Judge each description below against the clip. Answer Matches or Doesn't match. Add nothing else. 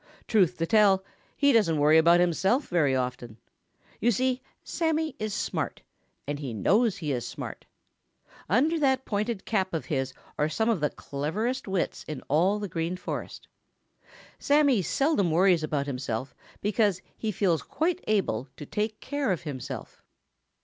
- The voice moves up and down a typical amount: Doesn't match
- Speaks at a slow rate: Doesn't match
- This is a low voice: Doesn't match